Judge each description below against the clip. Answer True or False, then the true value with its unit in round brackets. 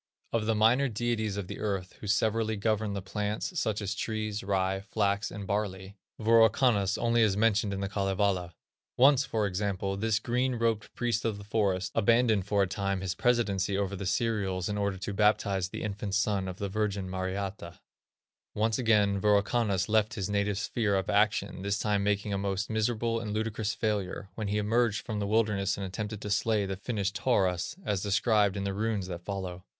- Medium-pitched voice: False (105 Hz)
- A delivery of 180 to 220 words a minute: True (190 wpm)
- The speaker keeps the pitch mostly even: True (2.0 semitones)